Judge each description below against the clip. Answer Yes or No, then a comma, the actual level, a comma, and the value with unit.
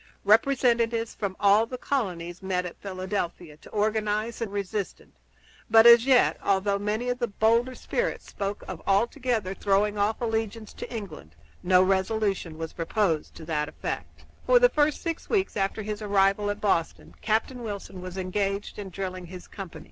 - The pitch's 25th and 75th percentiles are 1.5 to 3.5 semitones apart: Yes, average, 3.2 semitones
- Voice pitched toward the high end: Yes, high, 205 Hz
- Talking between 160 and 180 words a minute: Yes, average, 165 wpm